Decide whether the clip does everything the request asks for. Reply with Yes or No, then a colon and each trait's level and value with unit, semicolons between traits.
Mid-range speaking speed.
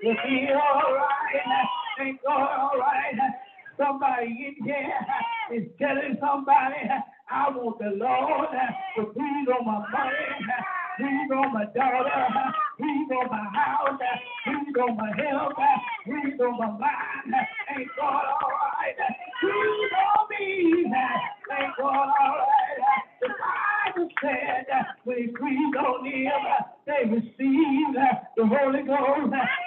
No: slow, 130 wpm